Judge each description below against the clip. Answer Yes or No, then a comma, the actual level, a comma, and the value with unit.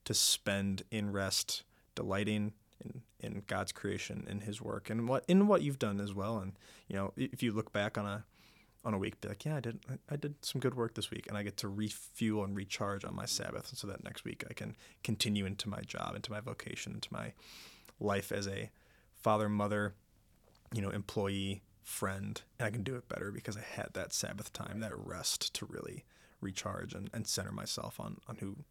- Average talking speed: No, fast, 215 wpm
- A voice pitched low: Yes, low, 105 Hz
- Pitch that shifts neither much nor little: No, narrow, 2.2 semitones